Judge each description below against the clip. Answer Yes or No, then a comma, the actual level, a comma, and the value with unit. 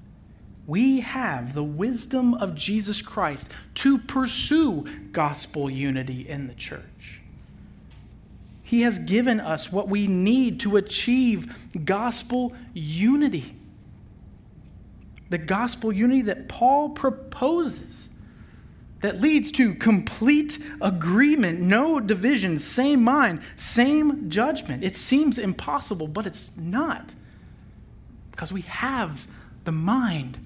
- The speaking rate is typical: No, slow, 105 wpm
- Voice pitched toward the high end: Yes, high, 205 Hz